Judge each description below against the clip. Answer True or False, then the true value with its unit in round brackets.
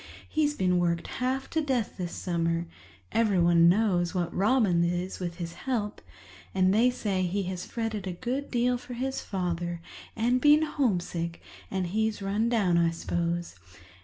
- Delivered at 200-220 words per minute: False (150 wpm)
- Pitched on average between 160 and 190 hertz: True (185 Hz)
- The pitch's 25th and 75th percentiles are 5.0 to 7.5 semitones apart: True (5.4 semitones)